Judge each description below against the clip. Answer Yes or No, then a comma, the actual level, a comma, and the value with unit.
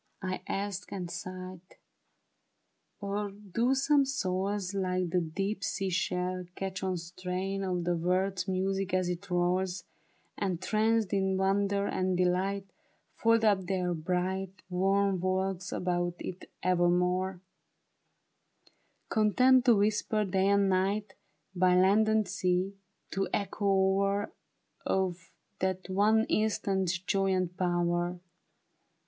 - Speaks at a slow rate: Yes, slow, 125 wpm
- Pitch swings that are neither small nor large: No, narrow, 1.7 semitones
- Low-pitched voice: No, high, 190 Hz